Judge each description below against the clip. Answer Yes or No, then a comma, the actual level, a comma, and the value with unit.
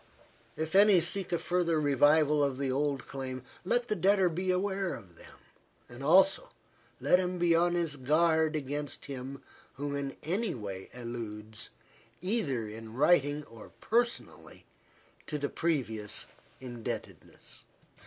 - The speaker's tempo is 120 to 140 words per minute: Yes, slow, 135 wpm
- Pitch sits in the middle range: Yes, medium, 150 Hz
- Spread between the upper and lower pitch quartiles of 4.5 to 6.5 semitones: Yes, wide, 5.4 semitones